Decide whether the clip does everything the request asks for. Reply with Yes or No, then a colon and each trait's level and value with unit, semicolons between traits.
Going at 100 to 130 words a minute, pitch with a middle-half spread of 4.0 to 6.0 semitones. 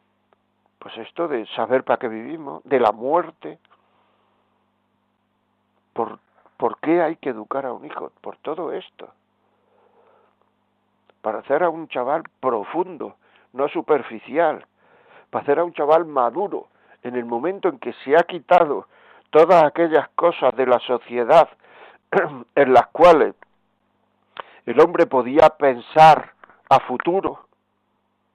Yes: slow, 125 wpm; wide, 5.4 semitones